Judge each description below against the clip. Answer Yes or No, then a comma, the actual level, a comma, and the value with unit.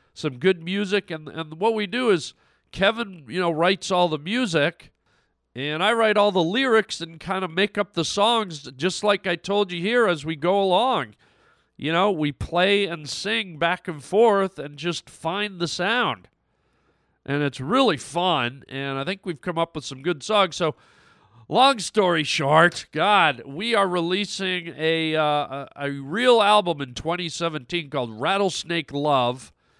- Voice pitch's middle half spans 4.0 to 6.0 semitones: Yes, average, 4.6 semitones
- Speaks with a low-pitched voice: No, medium, 175 Hz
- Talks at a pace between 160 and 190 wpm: Yes, average, 175 wpm